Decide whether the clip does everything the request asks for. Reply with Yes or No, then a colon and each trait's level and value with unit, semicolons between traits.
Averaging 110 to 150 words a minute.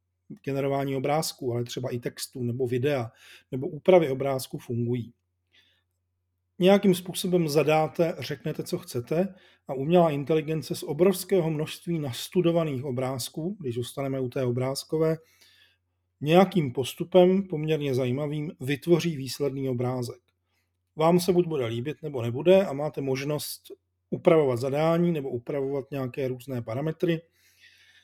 Yes: average, 120 wpm